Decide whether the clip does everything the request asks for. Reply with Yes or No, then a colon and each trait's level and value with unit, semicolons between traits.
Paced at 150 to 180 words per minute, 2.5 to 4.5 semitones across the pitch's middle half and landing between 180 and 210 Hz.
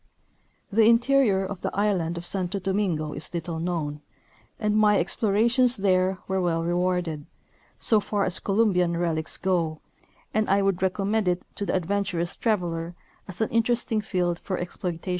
Yes: average, 160 wpm; average, 3.2 semitones; high, 190 Hz